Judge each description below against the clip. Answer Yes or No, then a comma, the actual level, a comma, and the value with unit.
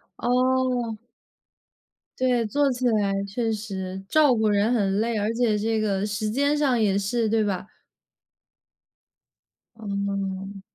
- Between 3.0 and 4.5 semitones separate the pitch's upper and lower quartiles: Yes, average, 3.5 semitones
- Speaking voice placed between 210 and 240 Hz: Yes, high, 215 Hz